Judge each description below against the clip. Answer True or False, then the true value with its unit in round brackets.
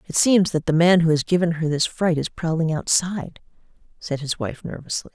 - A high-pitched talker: False (165 Hz)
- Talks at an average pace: False (210 wpm)